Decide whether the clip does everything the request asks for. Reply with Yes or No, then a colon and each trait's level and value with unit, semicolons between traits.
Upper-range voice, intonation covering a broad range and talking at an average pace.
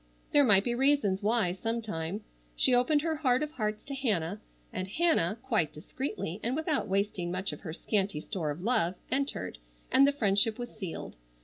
Yes: high, 215 Hz; wide, 6.1 semitones; average, 180 wpm